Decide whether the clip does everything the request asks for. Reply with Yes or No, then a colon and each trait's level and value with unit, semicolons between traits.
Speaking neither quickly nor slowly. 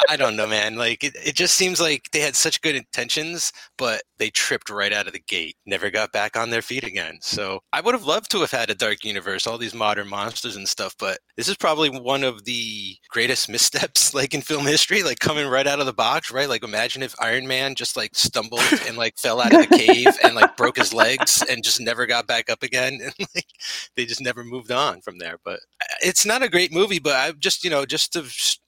No: fast, 245 wpm